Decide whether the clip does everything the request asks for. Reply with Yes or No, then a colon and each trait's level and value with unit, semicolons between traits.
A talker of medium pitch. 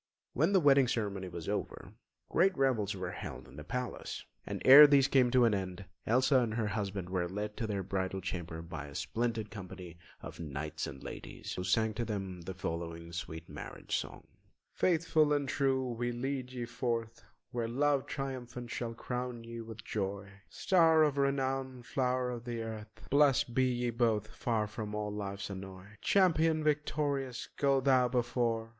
No: low, 115 Hz